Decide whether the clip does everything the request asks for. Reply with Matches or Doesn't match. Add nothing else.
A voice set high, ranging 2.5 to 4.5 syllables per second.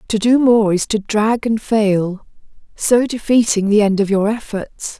Matches